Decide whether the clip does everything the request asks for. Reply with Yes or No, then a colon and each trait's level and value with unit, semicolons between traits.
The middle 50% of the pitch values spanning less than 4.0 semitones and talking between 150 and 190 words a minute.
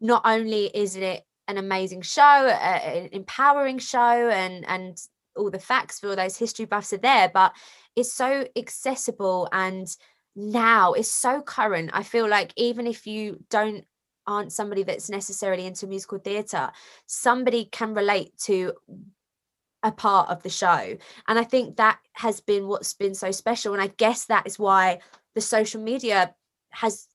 Yes: average, 3.3 semitones; average, 165 wpm